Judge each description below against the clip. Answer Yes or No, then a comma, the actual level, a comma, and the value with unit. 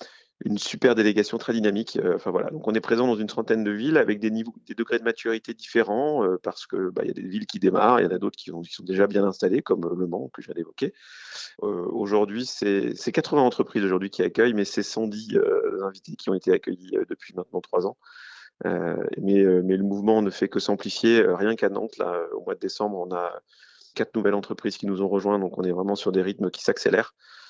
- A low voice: Yes, low, 105 Hz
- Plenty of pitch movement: No, average, 3.5 semitones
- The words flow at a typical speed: No, fast, 245 wpm